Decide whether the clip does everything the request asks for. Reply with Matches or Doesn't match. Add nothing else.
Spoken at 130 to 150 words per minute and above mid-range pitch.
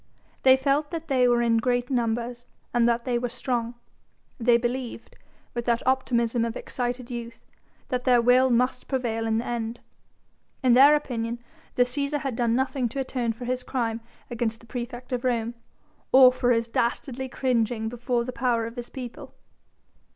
Doesn't match